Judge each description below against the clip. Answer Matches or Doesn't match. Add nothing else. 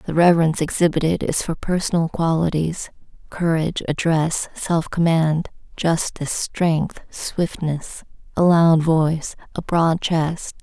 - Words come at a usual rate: Doesn't match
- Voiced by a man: Doesn't match